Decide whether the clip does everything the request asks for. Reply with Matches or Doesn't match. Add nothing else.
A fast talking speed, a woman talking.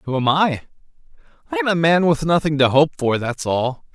Doesn't match